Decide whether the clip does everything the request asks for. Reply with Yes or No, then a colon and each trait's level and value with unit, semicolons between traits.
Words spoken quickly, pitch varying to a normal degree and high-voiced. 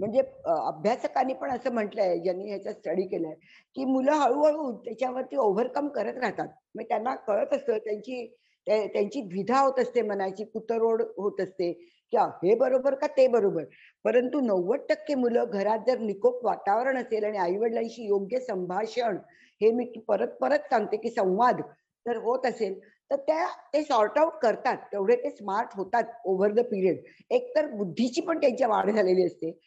Yes: fast, 160 wpm; average, 4.6 semitones; high, 235 Hz